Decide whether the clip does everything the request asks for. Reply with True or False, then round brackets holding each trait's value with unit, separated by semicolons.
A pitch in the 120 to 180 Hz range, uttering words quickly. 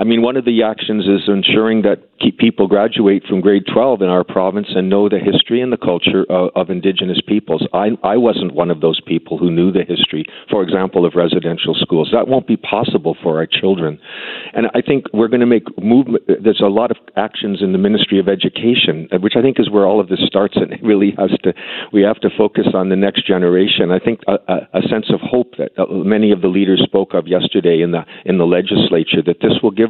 False (100 Hz; 235 wpm)